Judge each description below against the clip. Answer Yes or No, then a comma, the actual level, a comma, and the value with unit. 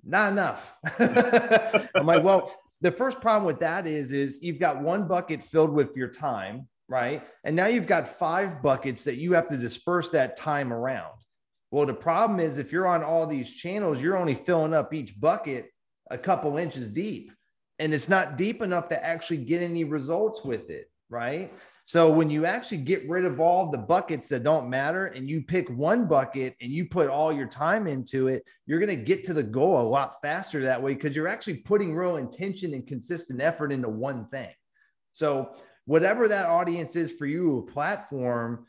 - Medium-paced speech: Yes, average, 195 wpm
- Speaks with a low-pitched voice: No, medium, 165 Hz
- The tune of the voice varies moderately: Yes, average, 4.8 semitones